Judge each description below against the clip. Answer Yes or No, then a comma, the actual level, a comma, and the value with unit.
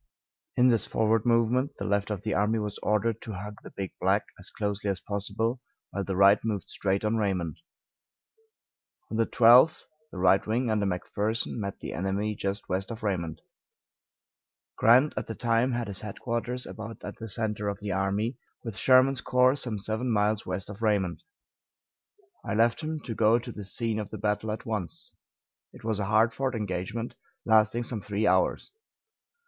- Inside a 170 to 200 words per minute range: Yes, average, 180 wpm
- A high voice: No, low, 110 Hz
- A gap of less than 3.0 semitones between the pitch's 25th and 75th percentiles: Yes, narrow, 2.5 semitones